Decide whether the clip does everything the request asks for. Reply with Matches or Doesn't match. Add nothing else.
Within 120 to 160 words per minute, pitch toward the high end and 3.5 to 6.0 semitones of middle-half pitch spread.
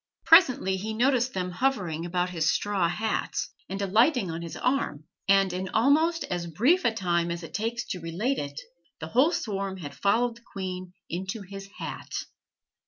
Doesn't match